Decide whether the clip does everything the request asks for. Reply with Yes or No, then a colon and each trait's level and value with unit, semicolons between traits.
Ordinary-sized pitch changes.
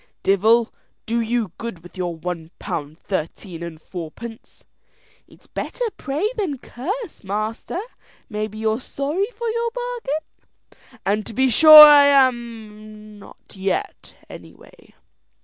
No: wide, 6.8 semitones